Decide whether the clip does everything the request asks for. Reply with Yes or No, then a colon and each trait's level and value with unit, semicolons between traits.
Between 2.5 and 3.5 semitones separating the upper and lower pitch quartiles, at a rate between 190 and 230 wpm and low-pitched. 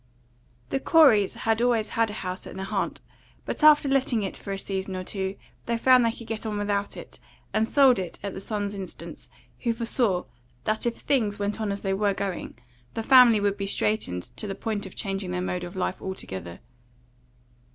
No: average, 3.0 semitones; average, 200 wpm; high, 205 Hz